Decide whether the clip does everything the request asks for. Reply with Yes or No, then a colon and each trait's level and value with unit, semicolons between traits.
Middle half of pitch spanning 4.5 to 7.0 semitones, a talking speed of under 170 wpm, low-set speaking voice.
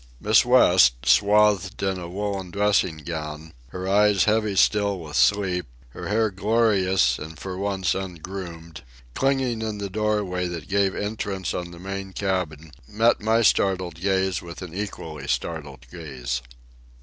No: average, 3.5 semitones; average, 150 wpm; very low, 95 Hz